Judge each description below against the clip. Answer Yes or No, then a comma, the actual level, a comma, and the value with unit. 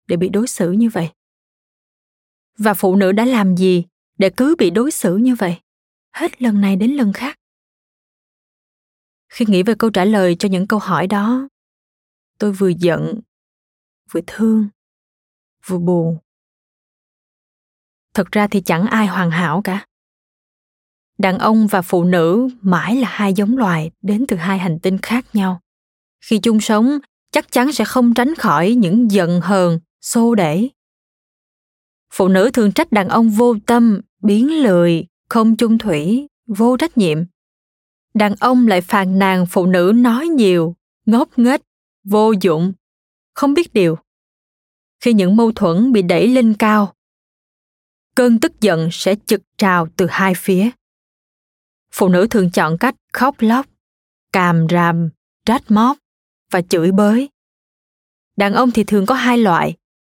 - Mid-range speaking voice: No, high, 205 Hz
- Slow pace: Yes, slow, 150 wpm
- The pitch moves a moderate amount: Yes, average, 4.2 semitones